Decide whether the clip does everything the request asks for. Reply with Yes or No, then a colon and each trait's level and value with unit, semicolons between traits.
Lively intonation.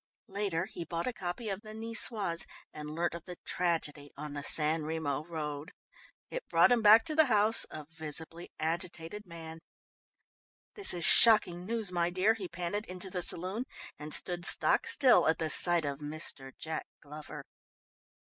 No: average, 4.6 semitones